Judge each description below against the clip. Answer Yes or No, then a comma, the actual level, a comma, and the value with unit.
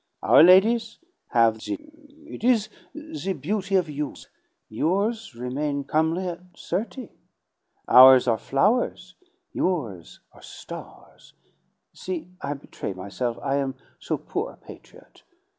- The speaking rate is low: Yes, slow, 120 wpm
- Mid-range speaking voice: Yes, medium, 165 Hz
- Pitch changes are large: Yes, wide, 7.1 semitones